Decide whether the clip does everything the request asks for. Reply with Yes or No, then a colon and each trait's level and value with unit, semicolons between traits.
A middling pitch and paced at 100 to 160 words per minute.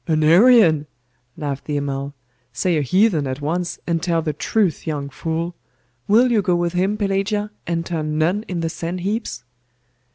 No: medium, 170 Hz; average, 170 wpm